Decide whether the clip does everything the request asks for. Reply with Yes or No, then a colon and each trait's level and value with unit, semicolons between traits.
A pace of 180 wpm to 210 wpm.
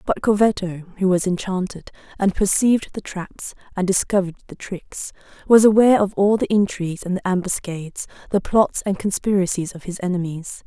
No: average, 165 wpm